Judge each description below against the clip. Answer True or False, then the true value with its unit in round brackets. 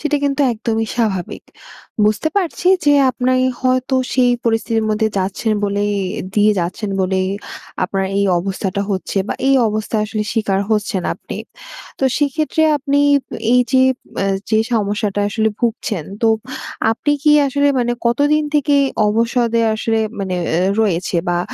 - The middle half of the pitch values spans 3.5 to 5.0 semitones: True (4.2 semitones)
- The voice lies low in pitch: False (225 Hz)